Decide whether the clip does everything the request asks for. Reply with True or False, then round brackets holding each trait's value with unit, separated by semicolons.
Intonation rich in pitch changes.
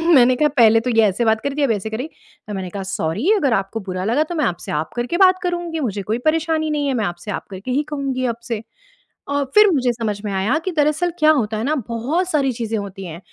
True (6.3 semitones)